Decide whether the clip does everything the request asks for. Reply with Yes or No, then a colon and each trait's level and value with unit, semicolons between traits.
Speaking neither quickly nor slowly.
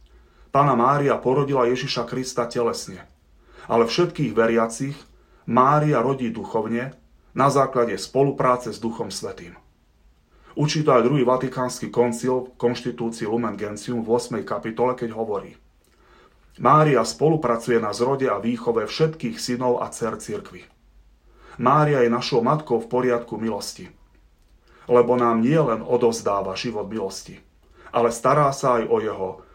Yes: average, 130 wpm